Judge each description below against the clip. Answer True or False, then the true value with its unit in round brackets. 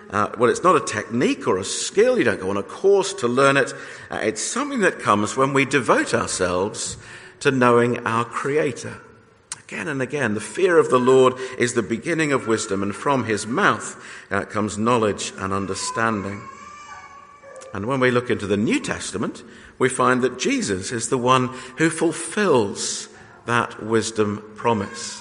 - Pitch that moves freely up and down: True (6.5 semitones)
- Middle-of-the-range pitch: False (130 Hz)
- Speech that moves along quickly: False (175 wpm)